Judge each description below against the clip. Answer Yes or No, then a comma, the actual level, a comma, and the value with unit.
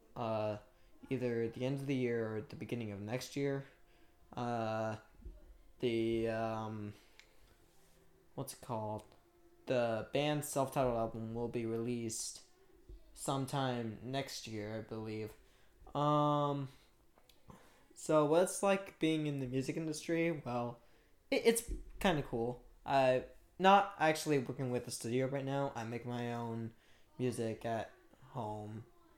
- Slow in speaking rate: Yes, slow, 130 wpm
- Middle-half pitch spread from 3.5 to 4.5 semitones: Yes, average, 4.1 semitones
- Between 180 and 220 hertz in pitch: No, low, 125 Hz